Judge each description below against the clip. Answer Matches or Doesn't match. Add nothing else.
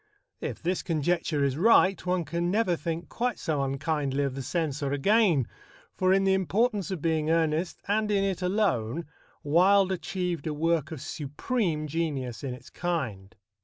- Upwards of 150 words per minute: Matches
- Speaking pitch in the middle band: Matches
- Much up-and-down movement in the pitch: Doesn't match